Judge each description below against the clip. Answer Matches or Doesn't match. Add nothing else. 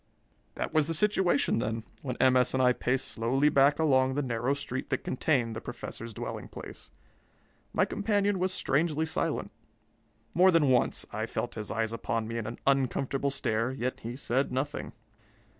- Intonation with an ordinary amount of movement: Matches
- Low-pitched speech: Matches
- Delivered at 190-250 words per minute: Doesn't match